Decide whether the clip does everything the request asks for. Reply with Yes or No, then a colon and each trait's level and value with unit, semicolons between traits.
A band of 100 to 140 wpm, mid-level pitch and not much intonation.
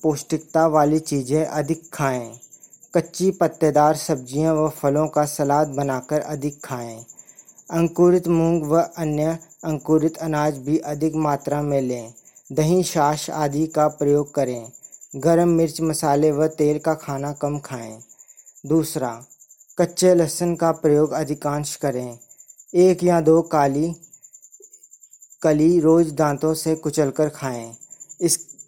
Yes: average, 125 wpm; medium, 155 Hz; narrow, 2.1 semitones